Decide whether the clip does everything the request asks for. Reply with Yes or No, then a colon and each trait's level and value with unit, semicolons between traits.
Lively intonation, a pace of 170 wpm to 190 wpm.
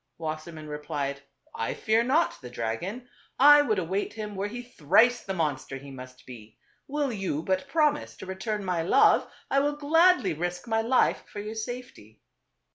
Yes: wide, 8.4 semitones; average, 175 wpm